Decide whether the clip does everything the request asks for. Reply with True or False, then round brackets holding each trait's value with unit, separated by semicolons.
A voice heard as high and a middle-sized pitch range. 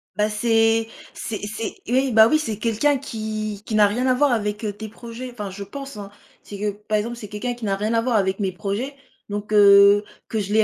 False (215 Hz; 2.3 semitones)